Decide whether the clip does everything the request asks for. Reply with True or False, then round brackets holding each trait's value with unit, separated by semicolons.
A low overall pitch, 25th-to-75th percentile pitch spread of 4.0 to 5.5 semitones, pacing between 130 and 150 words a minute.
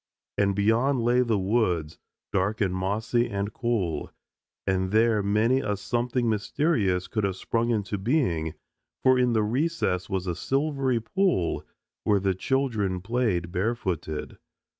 True (105 Hz; 4.4 semitones; 140 wpm)